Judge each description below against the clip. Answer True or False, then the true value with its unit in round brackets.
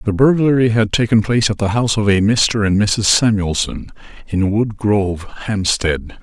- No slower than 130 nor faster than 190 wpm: True (175 wpm)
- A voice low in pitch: True (105 Hz)